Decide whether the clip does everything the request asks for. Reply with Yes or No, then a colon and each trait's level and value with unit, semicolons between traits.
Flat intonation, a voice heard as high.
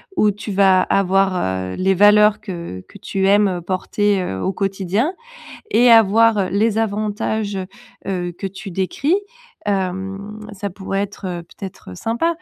Yes: narrow, 1.9 semitones; high, 195 Hz